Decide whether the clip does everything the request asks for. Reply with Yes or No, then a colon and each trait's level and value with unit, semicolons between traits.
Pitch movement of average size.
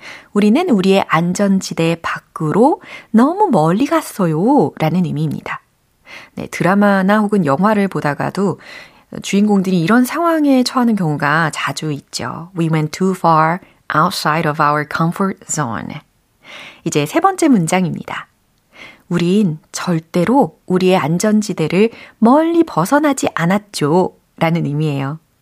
No: wide, 6.1 semitones